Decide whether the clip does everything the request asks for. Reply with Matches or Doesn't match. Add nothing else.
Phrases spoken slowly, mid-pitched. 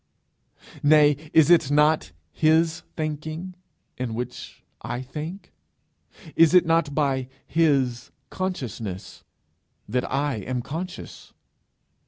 Matches